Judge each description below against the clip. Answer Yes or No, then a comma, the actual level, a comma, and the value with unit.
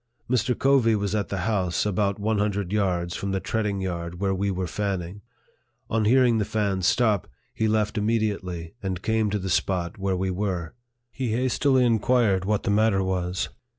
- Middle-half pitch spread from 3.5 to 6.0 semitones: No, average, 2.8 semitones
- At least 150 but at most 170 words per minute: No, average, 180 wpm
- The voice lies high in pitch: No, low, 100 Hz